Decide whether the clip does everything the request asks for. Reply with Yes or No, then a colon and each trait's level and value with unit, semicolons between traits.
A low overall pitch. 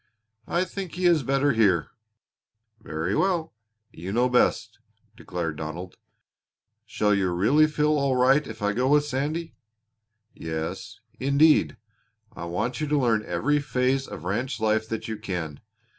Yes: low, 125 Hz